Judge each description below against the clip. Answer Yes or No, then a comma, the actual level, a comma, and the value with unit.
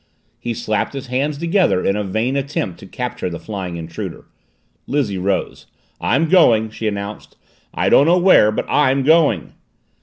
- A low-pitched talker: Yes, low, 120 Hz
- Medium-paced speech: Yes, average, 160 wpm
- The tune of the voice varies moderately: No, wide, 6.2 semitones